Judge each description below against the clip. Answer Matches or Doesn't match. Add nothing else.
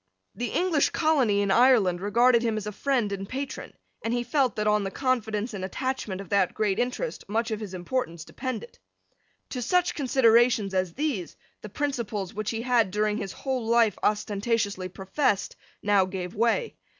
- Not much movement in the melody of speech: Doesn't match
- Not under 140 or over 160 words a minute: Doesn't match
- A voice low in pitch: Doesn't match